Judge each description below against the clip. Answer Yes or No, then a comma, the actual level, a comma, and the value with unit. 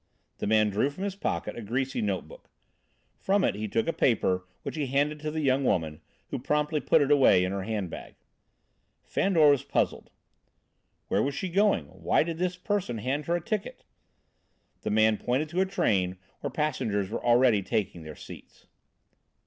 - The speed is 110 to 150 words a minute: No, average, 180 wpm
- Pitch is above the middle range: No, low, 130 Hz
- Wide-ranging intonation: Yes, wide, 6.9 semitones